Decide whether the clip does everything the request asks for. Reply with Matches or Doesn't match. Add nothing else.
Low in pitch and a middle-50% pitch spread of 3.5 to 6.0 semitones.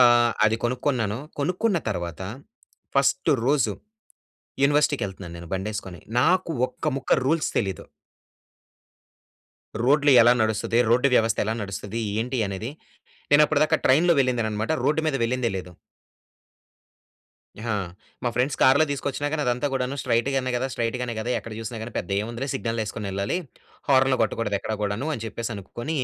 Matches